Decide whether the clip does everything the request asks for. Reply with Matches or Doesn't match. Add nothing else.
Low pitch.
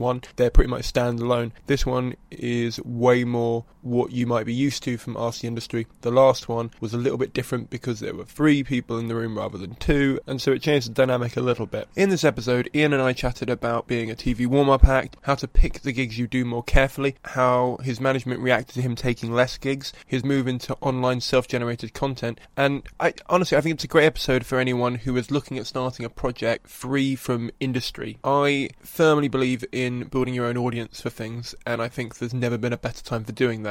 Matches